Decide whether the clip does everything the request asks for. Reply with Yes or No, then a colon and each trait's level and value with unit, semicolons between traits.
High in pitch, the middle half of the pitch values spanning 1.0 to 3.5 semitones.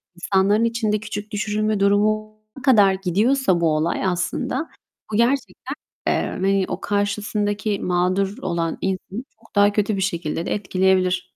Yes: high, 200 Hz; narrow, 2.5 semitones